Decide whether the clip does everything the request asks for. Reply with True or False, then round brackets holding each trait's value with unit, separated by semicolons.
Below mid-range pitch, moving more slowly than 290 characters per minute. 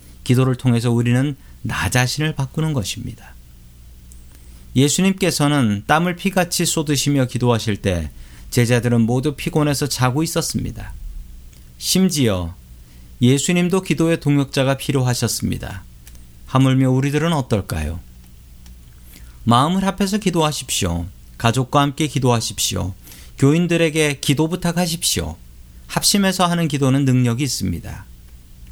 False (125 Hz; 295 characters per minute)